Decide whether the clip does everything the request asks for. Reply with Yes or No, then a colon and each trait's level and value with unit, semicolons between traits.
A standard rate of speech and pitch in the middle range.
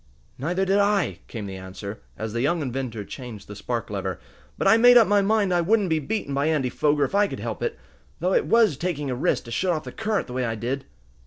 No: fast, 250 wpm; medium, 145 Hz